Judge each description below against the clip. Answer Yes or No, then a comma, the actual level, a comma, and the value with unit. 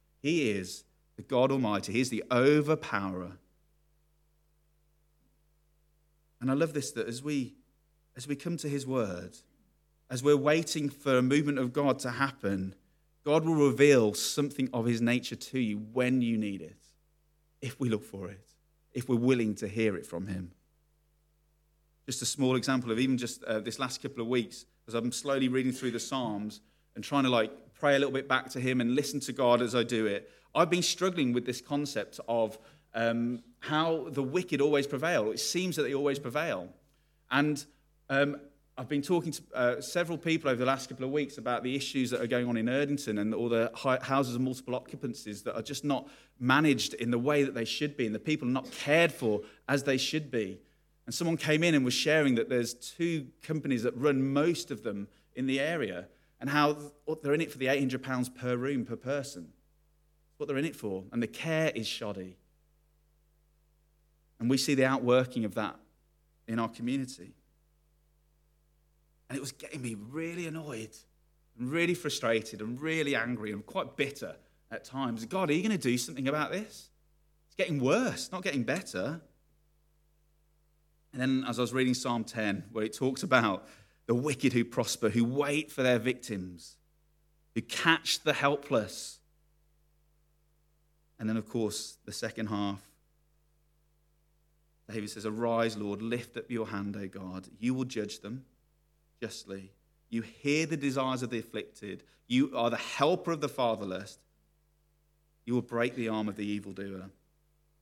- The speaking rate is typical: Yes, average, 180 wpm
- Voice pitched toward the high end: No, low, 135 Hz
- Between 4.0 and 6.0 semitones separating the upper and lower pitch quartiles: Yes, average, 4.5 semitones